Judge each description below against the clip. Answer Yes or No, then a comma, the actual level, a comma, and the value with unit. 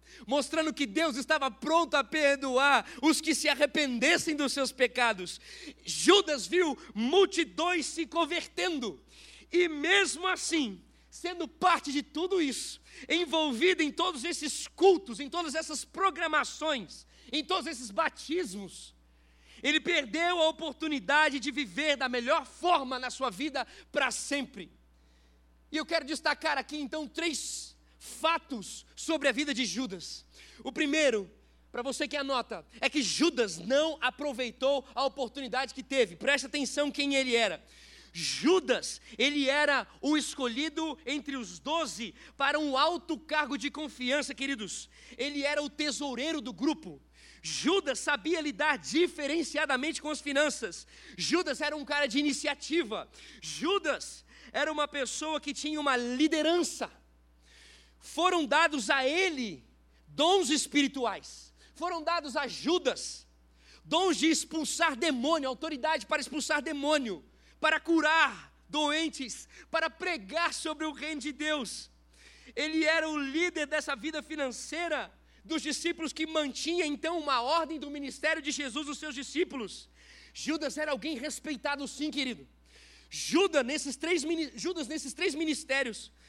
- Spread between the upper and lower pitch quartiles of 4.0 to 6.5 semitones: No, average, 3.2 semitones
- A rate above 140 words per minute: No, average, 135 wpm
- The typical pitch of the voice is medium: No, very high, 295 Hz